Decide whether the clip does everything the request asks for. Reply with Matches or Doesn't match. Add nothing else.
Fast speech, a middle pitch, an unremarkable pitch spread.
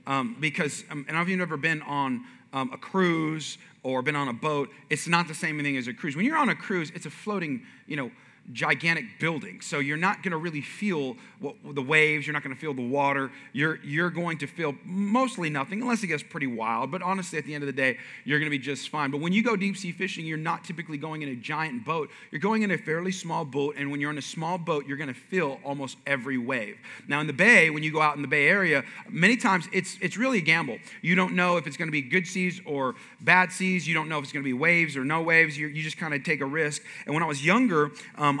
Matches